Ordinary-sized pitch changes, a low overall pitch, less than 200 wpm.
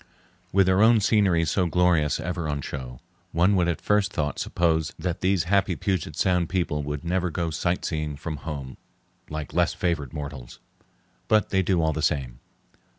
Yes: average, 3.6 semitones; very low, 85 Hz; average, 170 wpm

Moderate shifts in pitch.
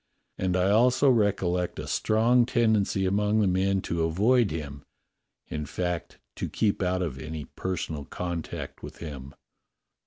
Yes: average, 4.6 semitones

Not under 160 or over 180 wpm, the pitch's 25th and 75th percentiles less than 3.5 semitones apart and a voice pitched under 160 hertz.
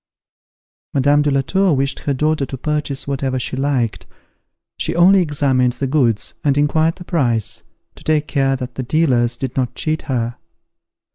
Yes: average, 165 wpm; average, 2.9 semitones; medium, 140 Hz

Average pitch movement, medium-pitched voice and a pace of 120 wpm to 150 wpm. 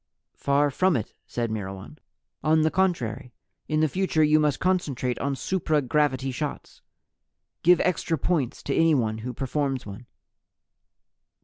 Yes: average, 4.2 semitones; medium, 145 Hz; slow, 135 wpm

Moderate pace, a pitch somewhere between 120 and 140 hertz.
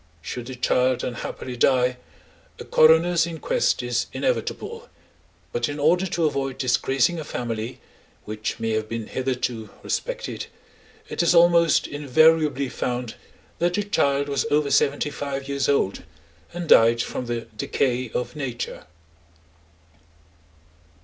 No: slow, 130 wpm; low, 135 Hz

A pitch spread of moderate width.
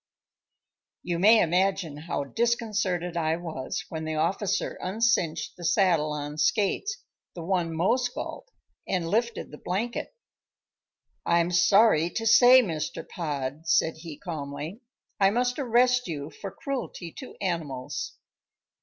No: wide, 5.8 semitones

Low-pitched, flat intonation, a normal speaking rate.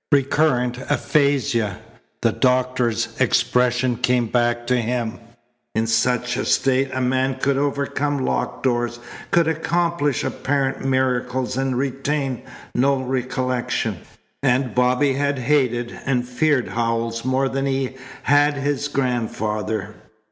No: low, 130 Hz; narrow, 2.1 semitones; slow, 120 wpm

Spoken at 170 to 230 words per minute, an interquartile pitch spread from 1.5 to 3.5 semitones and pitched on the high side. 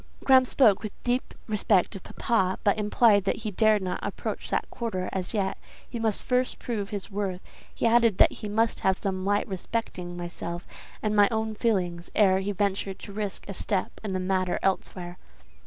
Yes: average, 190 wpm; average, 2.8 semitones; high, 200 Hz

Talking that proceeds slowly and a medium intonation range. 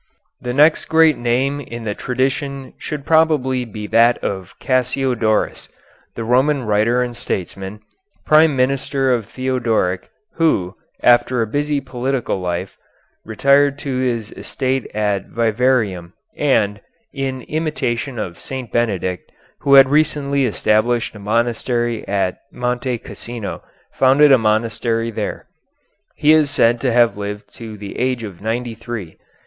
Yes: slow, 130 wpm; average, 3.8 semitones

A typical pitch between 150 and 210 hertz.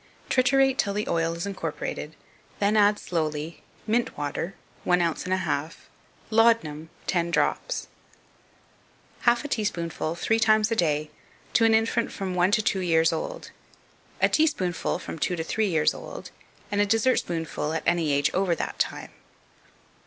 Yes: medium, 185 Hz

